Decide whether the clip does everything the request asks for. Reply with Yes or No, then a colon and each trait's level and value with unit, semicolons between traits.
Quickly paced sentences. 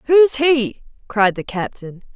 No: average, 140 wpm